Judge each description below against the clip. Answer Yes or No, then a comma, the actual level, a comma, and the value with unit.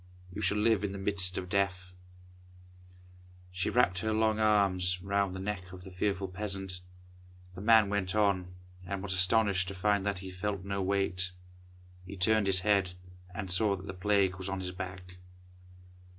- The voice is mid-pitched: No, very low, 95 Hz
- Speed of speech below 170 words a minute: No, average, 175 wpm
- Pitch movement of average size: No, narrow, 1.8 semitones